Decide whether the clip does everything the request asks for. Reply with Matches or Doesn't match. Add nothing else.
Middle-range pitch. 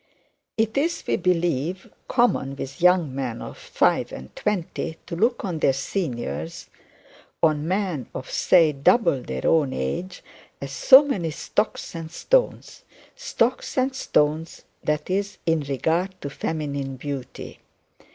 Matches